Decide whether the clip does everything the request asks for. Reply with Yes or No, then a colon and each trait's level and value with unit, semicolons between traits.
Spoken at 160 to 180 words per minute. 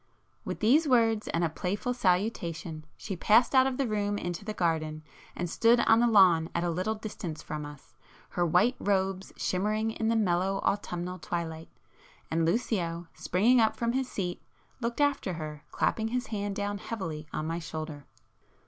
Yes: average, 170 wpm